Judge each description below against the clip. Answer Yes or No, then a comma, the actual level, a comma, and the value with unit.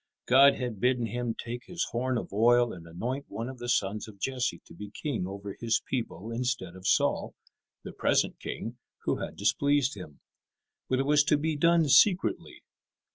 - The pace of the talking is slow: No, average, 185 wpm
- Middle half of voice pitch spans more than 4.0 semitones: Yes, average, 4.7 semitones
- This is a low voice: Yes, low, 120 Hz